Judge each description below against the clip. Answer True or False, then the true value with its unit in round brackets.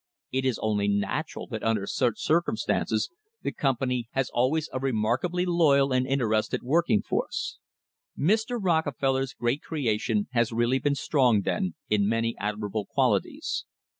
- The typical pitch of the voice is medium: False (130 Hz)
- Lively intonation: True (5.9 semitones)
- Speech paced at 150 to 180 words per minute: False (135 wpm)